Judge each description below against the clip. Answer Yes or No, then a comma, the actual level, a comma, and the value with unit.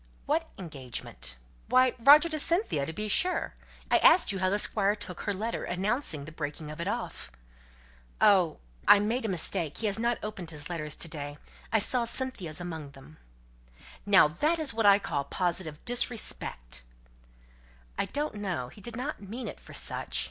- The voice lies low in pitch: No, high, 195 Hz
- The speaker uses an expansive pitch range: Yes, wide, 7.1 semitones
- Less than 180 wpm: Yes, average, 170 wpm